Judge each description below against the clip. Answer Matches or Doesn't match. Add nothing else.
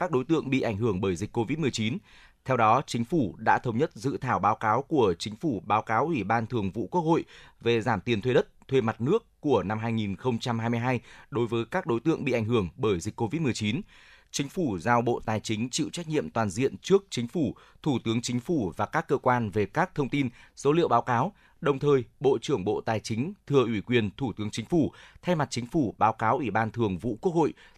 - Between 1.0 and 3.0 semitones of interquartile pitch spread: Doesn't match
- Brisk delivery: Doesn't match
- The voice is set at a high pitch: Doesn't match